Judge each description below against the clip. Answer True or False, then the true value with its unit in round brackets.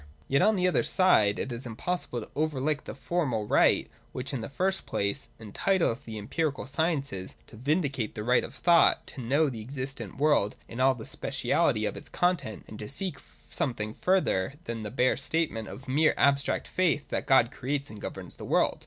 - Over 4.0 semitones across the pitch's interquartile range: True (5.5 semitones)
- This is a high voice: False (135 Hz)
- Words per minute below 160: False (195 wpm)